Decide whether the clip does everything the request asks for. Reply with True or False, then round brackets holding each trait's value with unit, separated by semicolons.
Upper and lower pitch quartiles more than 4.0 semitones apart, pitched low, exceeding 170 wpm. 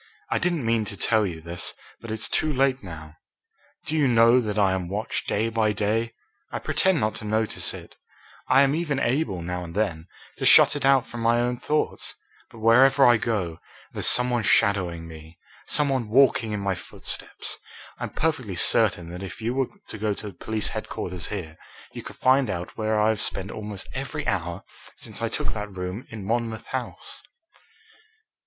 True (4.4 semitones; 110 Hz; 190 wpm)